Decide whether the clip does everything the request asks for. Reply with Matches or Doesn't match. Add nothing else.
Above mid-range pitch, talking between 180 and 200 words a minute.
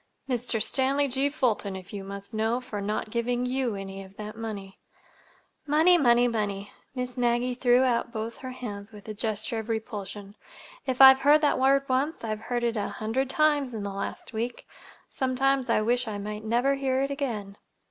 Matches